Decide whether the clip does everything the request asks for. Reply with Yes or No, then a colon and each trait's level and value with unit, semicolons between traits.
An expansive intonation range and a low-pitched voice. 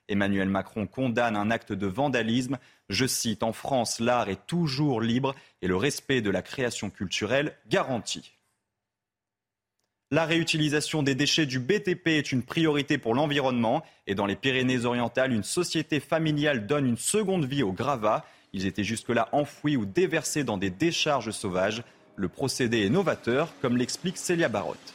Yes: wide, 6.5 semitones; low, 125 Hz